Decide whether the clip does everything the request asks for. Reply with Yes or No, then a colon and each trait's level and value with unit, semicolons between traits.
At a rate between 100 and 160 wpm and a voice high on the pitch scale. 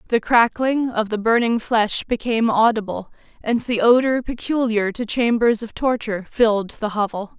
Yes: average, 155 wpm; high, 225 Hz